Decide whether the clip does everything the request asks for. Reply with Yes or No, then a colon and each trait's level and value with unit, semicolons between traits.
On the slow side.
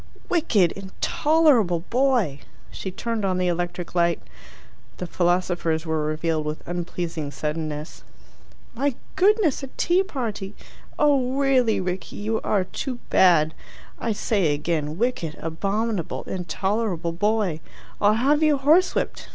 Yes: slow, 120 wpm